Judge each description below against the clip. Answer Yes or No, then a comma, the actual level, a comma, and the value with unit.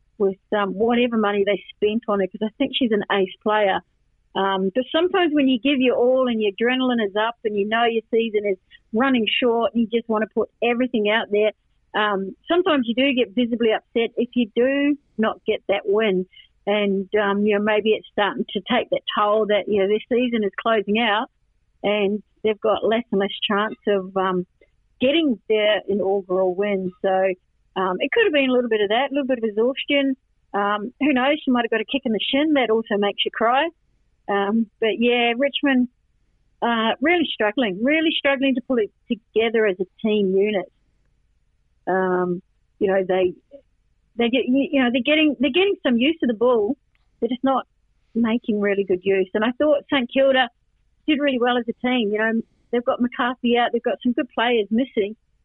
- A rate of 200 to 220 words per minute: Yes, fast, 205 wpm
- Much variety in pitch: No, average, 4.0 semitones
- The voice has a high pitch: Yes, high, 225 Hz